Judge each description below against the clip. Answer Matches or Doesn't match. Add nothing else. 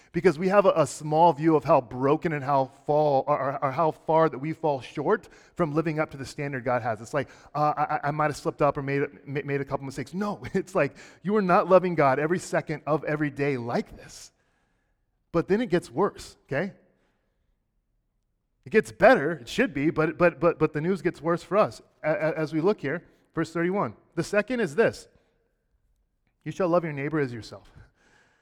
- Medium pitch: Matches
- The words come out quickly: Matches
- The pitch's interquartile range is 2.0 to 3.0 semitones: Doesn't match